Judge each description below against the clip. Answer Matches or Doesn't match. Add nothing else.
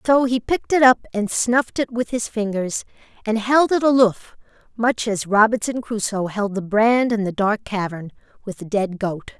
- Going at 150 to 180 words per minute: Doesn't match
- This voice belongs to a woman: Matches